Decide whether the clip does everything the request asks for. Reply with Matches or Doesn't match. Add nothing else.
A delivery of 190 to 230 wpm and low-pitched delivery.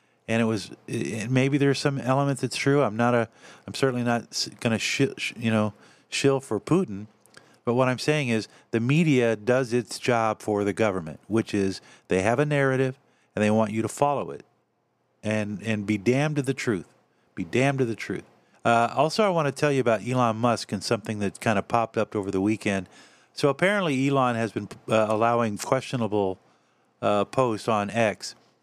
Matches